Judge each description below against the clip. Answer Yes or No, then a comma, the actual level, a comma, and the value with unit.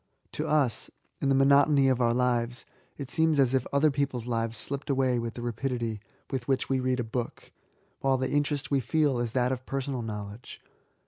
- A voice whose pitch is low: Yes, low, 130 Hz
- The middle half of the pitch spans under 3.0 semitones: Yes, narrow, 2.5 semitones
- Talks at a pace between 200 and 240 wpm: Yes, fast, 205 wpm